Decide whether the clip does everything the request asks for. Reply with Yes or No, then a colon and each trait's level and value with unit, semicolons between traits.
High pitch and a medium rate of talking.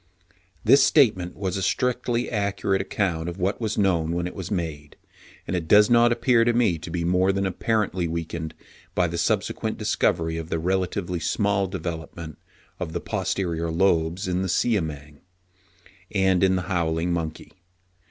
No: very low, 90 Hz; average, 160 wpm